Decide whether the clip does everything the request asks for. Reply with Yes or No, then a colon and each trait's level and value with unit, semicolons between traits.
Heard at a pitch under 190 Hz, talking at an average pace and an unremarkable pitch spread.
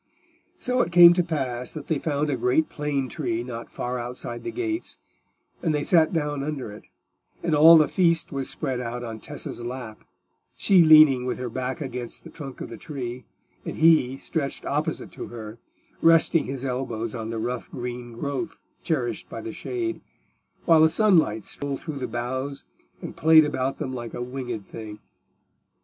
Yes: low, 135 Hz; average, 180 wpm; average, 4.5 semitones